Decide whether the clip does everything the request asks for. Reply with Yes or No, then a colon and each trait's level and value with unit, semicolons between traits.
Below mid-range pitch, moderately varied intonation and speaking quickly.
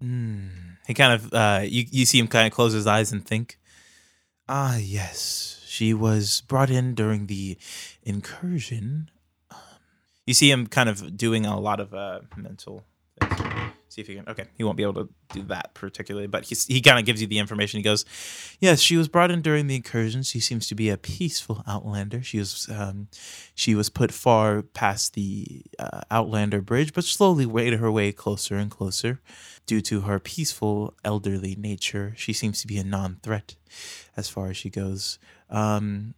No: low, 110 Hz; average, 3.0 semitones; average, 190 wpm